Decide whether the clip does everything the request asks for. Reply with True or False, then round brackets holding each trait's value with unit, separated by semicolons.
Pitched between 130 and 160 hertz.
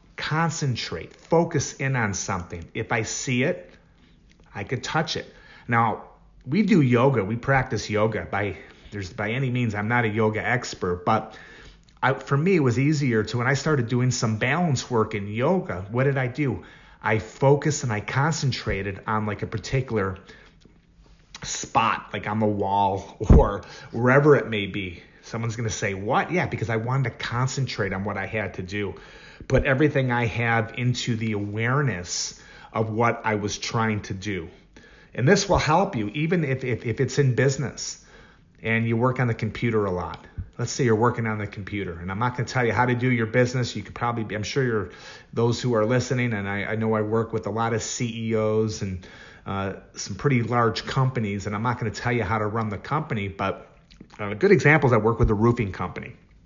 False (115 Hz)